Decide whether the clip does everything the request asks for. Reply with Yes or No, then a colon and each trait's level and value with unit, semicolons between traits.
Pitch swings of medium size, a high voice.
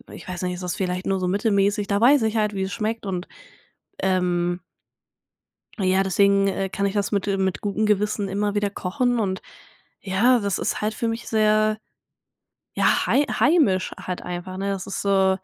No: narrow, 2.1 semitones; high, 200 Hz